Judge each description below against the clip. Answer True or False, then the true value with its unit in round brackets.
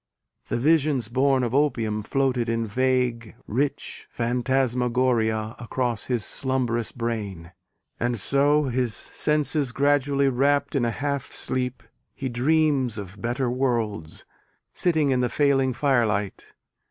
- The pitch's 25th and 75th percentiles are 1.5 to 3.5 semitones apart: True (2.9 semitones)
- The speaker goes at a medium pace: False (120 wpm)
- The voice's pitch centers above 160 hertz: False (125 Hz)